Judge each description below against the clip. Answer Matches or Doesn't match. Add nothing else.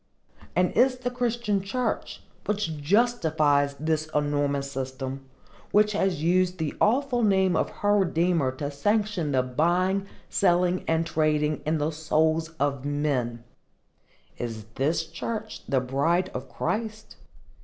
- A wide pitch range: Matches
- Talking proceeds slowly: Matches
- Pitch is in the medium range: Matches